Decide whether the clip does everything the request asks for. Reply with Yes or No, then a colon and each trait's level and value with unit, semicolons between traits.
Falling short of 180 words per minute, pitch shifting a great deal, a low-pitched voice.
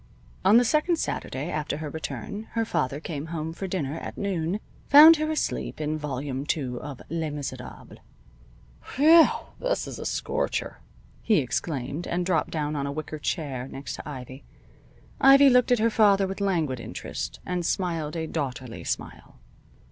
No: average, 165 wpm; wide, 6.0 semitones; medium, 160 Hz